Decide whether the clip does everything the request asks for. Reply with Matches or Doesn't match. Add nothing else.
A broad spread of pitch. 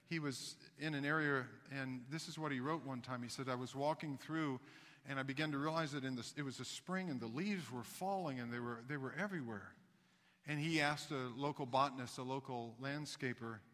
Doesn't match